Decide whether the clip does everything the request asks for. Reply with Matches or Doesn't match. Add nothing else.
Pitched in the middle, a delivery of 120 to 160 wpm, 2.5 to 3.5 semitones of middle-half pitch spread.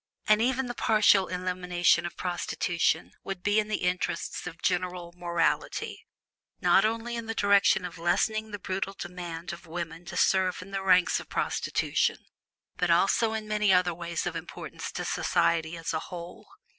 Doesn't match